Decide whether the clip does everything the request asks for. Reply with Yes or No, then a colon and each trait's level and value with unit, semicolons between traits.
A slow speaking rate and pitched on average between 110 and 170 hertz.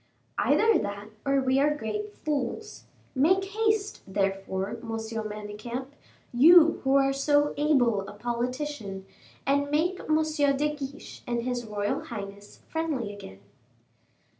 No: slow, 125 wpm; very high, 265 Hz